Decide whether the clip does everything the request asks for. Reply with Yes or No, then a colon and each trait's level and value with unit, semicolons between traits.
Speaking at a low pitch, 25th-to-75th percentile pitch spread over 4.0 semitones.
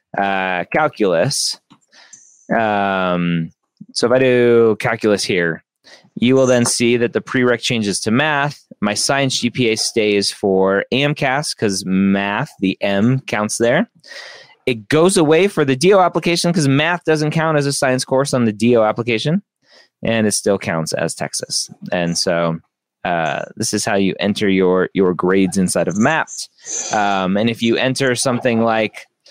Yes: low, 115 Hz; average, 5.2 semitones